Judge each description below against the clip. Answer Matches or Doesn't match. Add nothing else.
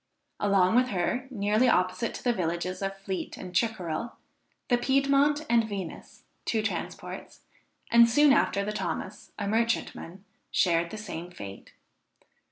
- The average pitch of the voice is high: Matches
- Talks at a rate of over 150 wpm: Doesn't match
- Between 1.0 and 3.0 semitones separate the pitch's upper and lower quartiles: Doesn't match